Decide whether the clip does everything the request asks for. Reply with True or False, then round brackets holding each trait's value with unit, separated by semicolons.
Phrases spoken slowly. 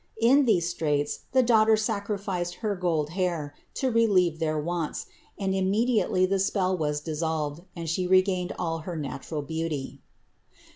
False (145 wpm)